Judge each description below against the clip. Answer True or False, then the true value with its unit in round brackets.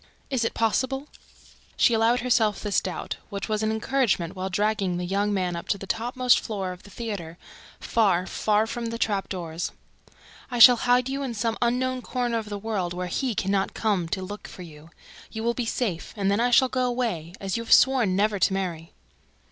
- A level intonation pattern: False (4.1 semitones)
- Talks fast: True (210 wpm)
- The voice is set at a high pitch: True (215 Hz)